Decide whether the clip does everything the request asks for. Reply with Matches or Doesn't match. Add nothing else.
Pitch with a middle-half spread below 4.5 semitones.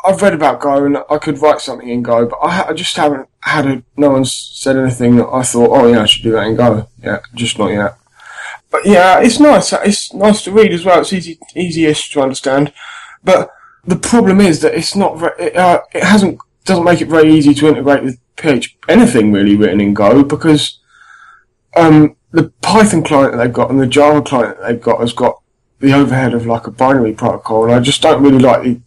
Doesn't match